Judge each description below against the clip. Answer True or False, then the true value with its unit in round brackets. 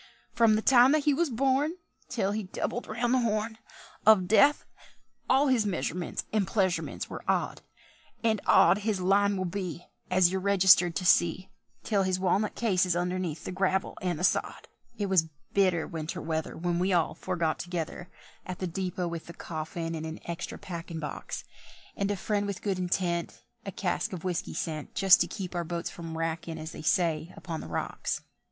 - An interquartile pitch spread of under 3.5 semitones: True (3.1 semitones)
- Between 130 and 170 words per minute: False (190 wpm)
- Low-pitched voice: False (185 Hz)